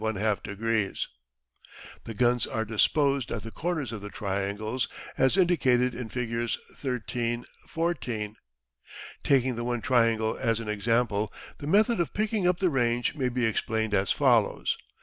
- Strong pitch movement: No, average, 3.4 semitones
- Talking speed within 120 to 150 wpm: Yes, average, 140 wpm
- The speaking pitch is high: No, low, 120 Hz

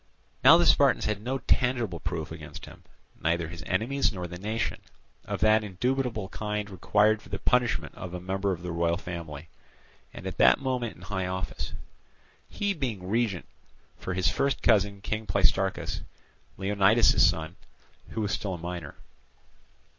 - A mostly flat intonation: No, average, 4.2 semitones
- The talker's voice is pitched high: No, low, 100 Hz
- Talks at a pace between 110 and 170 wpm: Yes, average, 155 wpm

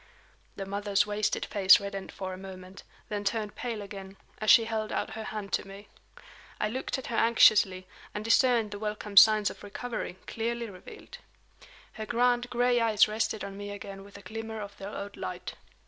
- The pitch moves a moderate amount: No, narrow, 2.1 semitones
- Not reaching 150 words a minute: No, average, 185 wpm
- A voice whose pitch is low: No, high, 210 Hz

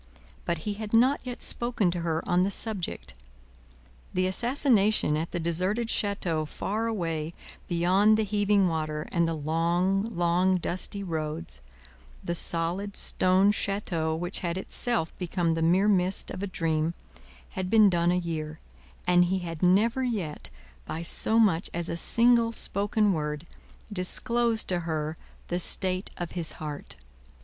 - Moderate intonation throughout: Yes, average, 3.7 semitones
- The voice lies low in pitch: No, medium, 180 Hz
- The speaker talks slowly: No, average, 150 wpm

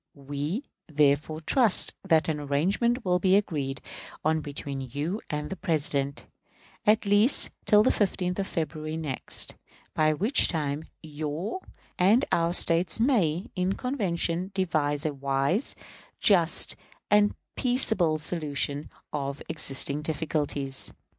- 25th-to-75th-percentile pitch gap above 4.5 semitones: Yes, average, 5.0 semitones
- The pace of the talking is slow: Yes, slow, 120 wpm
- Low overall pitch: No, medium, 160 Hz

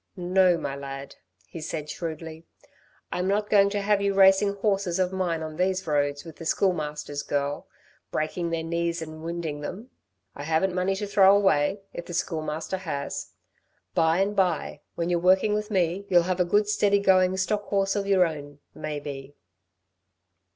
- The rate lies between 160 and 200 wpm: Yes, average, 170 wpm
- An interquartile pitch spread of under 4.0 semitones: Yes, average, 3.6 semitones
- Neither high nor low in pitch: Yes, medium, 175 Hz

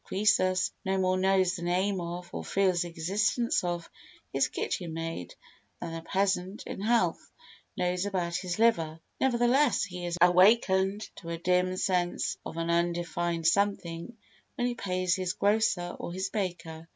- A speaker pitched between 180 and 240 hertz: Yes, medium, 185 Hz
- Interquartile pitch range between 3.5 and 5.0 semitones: No, narrow, 2.4 semitones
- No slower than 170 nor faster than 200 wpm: No, average, 155 wpm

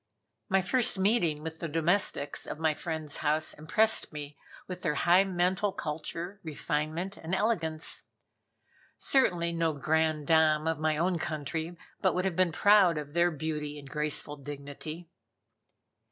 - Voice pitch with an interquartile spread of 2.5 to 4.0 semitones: Yes, average, 3.0 semitones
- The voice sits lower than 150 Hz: No, medium, 160 Hz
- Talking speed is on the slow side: No, average, 145 wpm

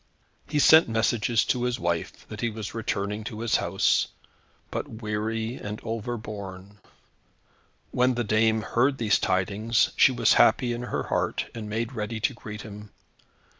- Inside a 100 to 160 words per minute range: Yes, average, 155 wpm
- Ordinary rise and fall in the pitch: No, narrow, 2.1 semitones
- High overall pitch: No, low, 110 Hz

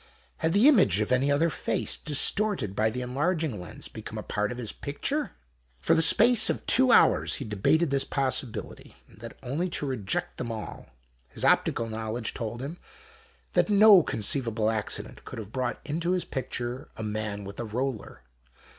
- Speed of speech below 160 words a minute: No, average, 175 wpm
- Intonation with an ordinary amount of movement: No, wide, 6.9 semitones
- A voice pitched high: No, low, 130 Hz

